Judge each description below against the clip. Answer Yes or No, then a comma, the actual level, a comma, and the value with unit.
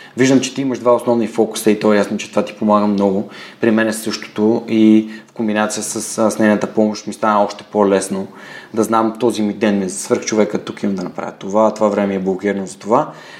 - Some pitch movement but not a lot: No, narrow, 1.3 semitones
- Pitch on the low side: Yes, low, 105 Hz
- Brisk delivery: Yes, fast, 225 wpm